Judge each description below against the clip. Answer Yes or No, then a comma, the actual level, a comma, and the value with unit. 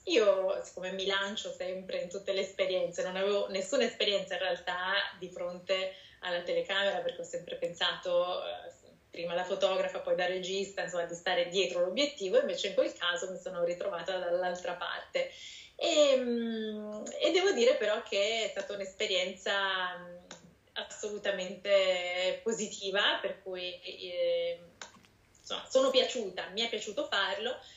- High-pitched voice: Yes, high, 195 Hz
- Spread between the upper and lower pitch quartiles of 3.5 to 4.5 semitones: Yes, average, 4.2 semitones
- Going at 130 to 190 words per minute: Yes, average, 140 wpm